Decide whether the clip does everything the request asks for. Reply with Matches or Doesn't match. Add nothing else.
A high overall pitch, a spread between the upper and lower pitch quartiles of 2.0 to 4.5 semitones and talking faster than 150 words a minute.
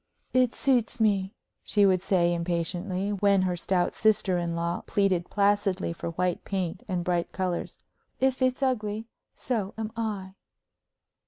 Doesn't match